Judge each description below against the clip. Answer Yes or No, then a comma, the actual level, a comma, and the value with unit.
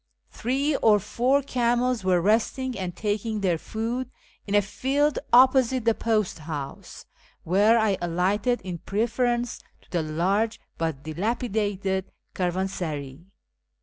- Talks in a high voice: Yes, high, 210 Hz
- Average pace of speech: No, slow, 120 wpm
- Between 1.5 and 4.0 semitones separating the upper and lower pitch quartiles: No, average, 5.0 semitones